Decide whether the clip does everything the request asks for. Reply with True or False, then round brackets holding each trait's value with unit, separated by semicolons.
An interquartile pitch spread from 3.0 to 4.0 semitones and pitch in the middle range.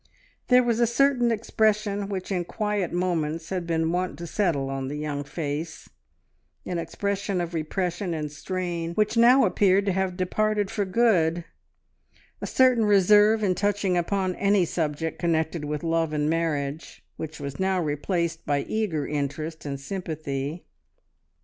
False (4.4 semitones; 175 Hz)